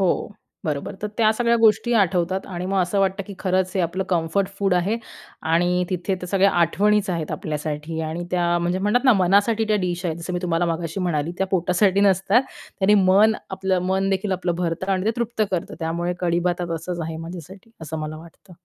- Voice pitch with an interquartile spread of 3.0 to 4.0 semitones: No, narrow, 2.4 semitones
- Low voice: No, medium, 180 Hz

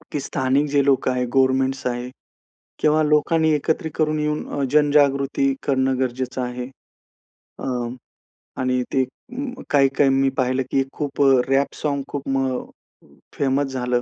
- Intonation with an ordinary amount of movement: No, narrow, 2.1 semitones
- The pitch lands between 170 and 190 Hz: No, low, 135 Hz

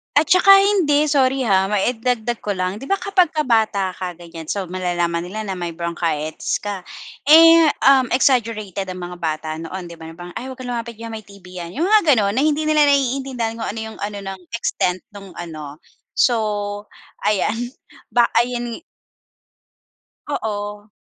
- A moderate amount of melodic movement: No, wide, 5.9 semitones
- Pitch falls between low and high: No, high, 210 Hz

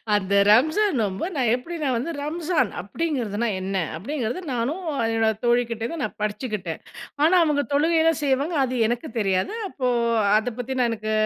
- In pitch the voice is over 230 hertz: Yes, high, 245 Hz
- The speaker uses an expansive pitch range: Yes, wide, 5.9 semitones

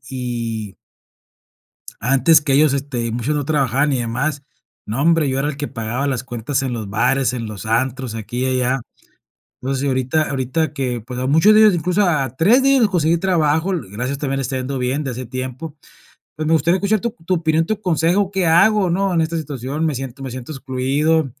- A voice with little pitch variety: No, average, 4.2 semitones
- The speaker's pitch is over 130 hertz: Yes, medium, 140 Hz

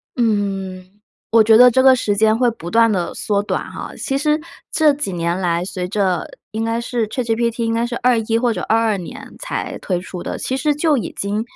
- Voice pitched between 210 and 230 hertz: Yes, high, 225 Hz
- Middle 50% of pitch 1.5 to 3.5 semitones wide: No, average, 3.9 semitones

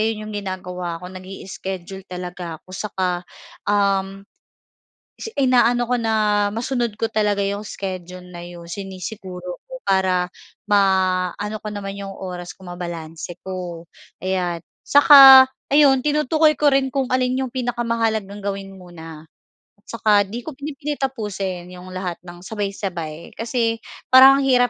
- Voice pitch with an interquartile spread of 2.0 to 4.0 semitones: No, average, 4.6 semitones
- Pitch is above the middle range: Yes, high, 200 Hz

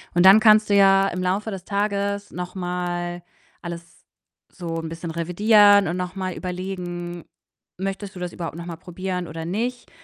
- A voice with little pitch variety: Yes, narrow, 2.3 semitones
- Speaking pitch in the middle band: Yes, medium, 180 Hz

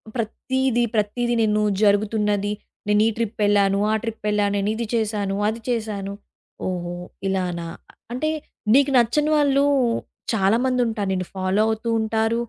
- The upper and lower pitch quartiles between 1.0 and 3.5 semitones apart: Yes, average, 2.7 semitones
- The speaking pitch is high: Yes, high, 215 Hz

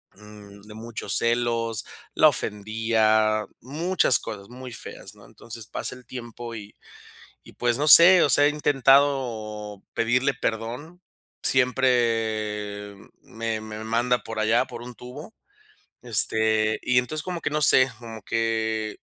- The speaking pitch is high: No, low, 115 Hz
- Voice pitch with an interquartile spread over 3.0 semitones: No, average, 2.7 semitones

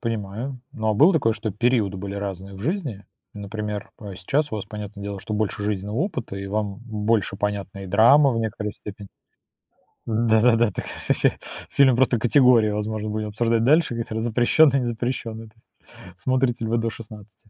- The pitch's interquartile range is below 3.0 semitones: Yes, narrow, 2.6 semitones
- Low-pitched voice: Yes, low, 110 Hz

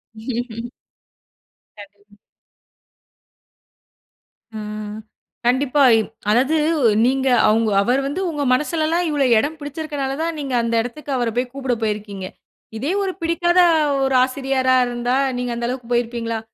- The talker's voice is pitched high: Yes, very high, 255 Hz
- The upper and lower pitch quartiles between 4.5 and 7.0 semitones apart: No, average, 3.9 semitones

